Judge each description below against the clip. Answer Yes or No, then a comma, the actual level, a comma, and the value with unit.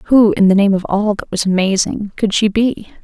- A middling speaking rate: No, fast, 240 wpm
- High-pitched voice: Yes, high, 205 Hz